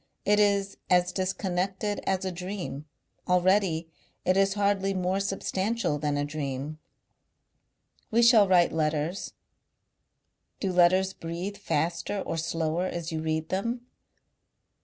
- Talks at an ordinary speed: No, slow, 120 wpm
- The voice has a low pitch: No, medium, 185 Hz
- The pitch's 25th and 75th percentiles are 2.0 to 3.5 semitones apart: Yes, average, 3.2 semitones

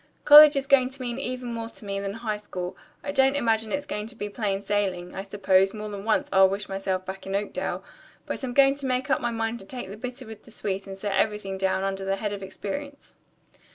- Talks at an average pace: No, fast, 250 wpm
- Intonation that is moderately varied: Yes, average, 4.4 semitones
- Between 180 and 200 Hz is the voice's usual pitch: No, high, 210 Hz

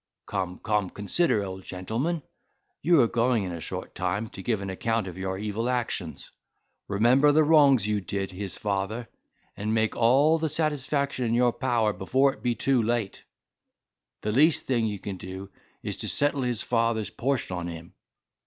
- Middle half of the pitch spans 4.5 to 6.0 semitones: Yes, average, 5.0 semitones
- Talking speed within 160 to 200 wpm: Yes, average, 175 wpm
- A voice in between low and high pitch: No, low, 115 Hz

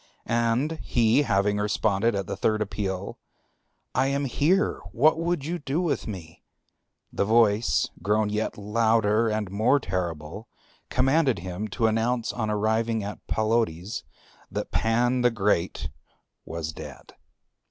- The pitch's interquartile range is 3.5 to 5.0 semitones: No, average, 3.1 semitones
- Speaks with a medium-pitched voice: No, low, 110 Hz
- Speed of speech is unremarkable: No, slow, 130 wpm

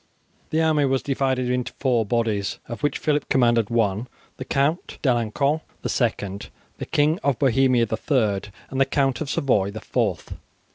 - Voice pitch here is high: No, low, 125 Hz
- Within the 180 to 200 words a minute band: No, average, 170 wpm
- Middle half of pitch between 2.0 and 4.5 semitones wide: Yes, average, 3.7 semitones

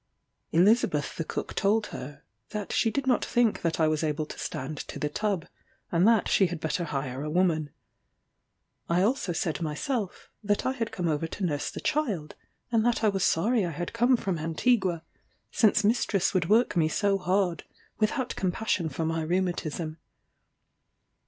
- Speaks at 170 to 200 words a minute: Yes, average, 175 wpm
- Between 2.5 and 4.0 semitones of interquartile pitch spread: No, wide, 5.4 semitones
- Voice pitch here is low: No, medium, 180 Hz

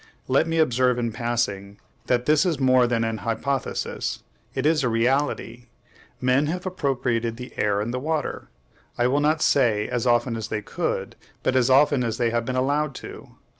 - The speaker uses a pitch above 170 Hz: No, low, 125 Hz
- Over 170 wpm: Yes, average, 185 wpm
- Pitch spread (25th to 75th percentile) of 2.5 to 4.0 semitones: Yes, average, 3.3 semitones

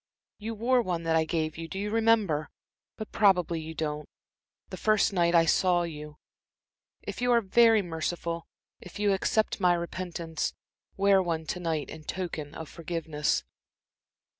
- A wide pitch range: No, average, 3.8 semitones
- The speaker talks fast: No, average, 160 wpm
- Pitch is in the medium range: Yes, medium, 175 Hz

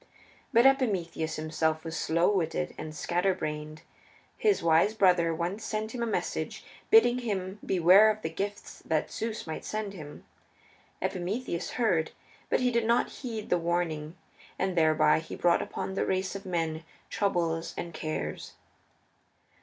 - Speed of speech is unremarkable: Yes, average, 150 wpm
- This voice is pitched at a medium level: Yes, medium, 180 Hz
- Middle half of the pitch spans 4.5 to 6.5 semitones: Yes, average, 4.8 semitones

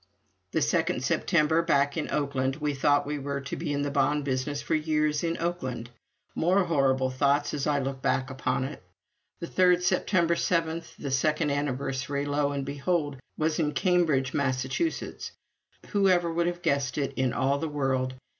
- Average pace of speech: Yes, average, 170 wpm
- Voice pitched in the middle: Yes, medium, 145 Hz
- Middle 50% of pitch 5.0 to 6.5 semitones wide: No, average, 3.3 semitones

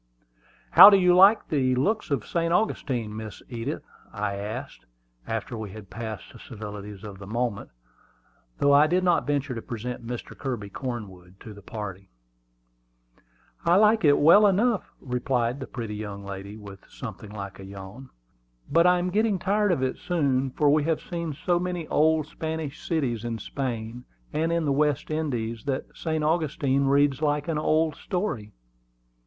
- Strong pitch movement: Yes, wide, 6.7 semitones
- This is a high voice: No, low, 135 Hz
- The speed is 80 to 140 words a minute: No, average, 170 wpm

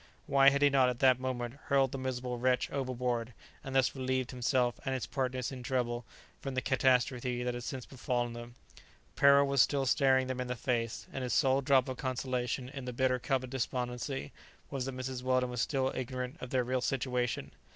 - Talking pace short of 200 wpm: No, fast, 205 wpm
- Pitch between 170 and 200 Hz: No, low, 130 Hz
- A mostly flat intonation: Yes, narrow, 1.3 semitones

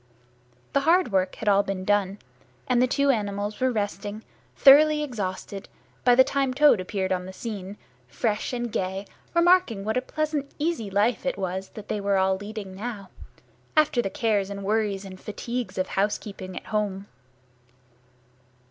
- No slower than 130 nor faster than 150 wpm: No, average, 160 wpm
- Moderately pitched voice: No, high, 210 Hz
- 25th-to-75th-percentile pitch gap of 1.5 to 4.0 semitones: No, average, 4.5 semitones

